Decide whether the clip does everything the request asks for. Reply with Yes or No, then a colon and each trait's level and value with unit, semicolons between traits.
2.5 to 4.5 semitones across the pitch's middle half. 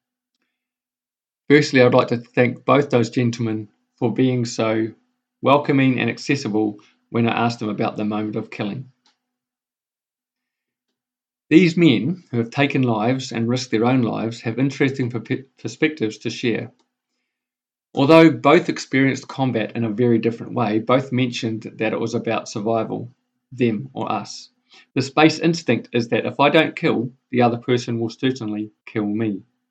Yes: average, 3.6 semitones